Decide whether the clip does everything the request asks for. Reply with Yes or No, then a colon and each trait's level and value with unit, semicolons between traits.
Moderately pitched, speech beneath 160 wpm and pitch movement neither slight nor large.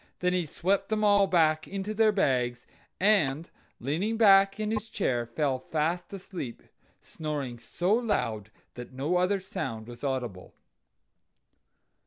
No: medium, 170 Hz; slow, 135 wpm; wide, 7.3 semitones